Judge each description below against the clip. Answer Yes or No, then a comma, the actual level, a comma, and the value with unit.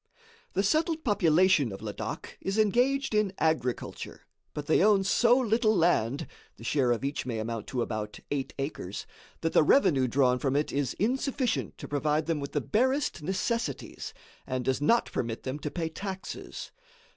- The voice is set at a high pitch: No, medium, 155 Hz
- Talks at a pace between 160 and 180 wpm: Yes, average, 170 wpm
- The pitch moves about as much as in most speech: No, wide, 8.2 semitones